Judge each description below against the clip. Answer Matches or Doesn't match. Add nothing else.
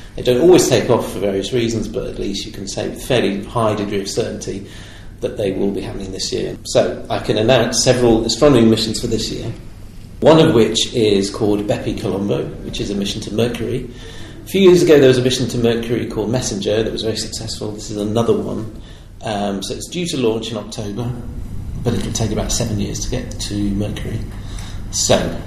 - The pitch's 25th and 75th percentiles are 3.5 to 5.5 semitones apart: Doesn't match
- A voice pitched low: Matches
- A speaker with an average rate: Doesn't match